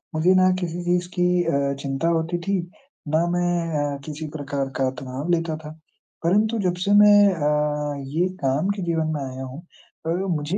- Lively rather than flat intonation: No, average, 3.7 semitones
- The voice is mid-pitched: Yes, medium, 165 Hz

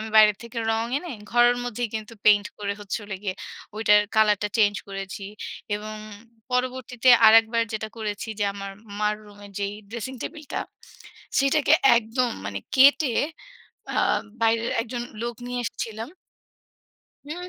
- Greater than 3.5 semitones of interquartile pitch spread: No, average, 2.8 semitones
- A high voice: Yes, high, 225 Hz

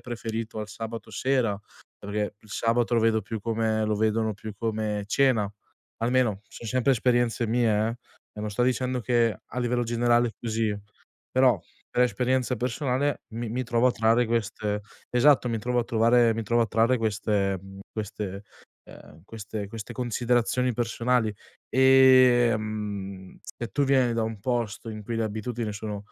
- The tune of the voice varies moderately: No, narrow, 2.2 semitones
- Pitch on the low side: Yes, low, 115 Hz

